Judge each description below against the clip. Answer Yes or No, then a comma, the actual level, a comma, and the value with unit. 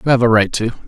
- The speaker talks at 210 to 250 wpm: No, fast, 345 wpm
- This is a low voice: Yes, low, 115 Hz